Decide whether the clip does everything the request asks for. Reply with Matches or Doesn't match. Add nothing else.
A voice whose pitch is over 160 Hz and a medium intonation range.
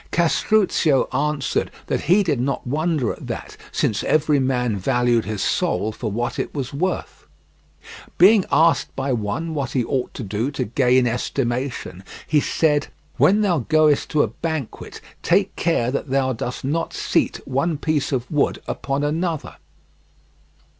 Doesn't match